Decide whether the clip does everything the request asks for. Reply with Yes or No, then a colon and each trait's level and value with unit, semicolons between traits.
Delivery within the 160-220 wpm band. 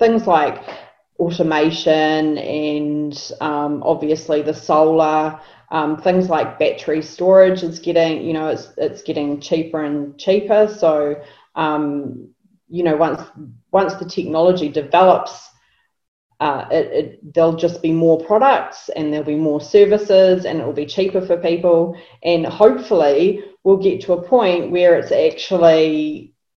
No: average, 140 wpm